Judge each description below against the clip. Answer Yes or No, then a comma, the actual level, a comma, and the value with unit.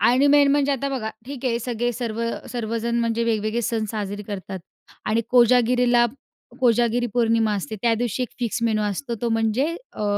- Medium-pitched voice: No, high, 235 Hz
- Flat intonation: Yes, narrow, 2.0 semitones